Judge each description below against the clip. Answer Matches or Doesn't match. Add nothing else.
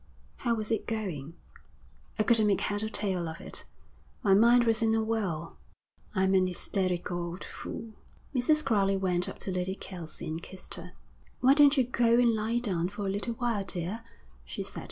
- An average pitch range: Matches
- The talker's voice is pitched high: Matches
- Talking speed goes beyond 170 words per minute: Matches